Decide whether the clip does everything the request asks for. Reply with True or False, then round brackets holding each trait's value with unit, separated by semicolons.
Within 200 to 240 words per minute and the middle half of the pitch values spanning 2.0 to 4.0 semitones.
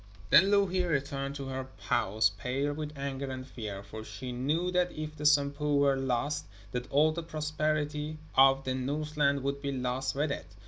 False (180 wpm; 2.6 semitones)